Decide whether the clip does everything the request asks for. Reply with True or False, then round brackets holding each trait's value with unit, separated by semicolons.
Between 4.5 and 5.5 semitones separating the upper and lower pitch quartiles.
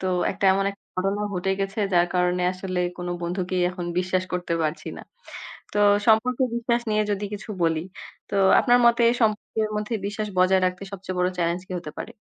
False (2.7 semitones)